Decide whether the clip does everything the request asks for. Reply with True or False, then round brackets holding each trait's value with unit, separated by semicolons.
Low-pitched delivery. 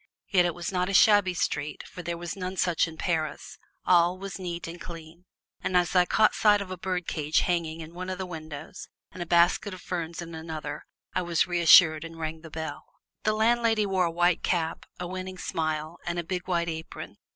False (175 Hz)